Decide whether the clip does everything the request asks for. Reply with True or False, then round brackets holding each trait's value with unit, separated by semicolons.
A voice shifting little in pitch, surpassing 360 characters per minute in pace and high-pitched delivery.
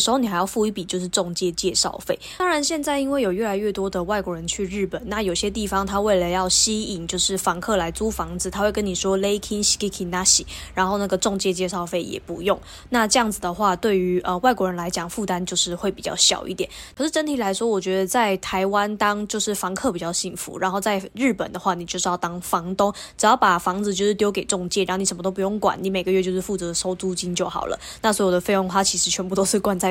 True (2.3 semitones; 375 characters per minute; 195 Hz)